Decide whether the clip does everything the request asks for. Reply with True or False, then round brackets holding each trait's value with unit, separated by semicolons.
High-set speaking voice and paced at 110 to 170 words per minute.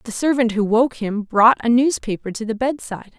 False (230 Hz; 205 wpm)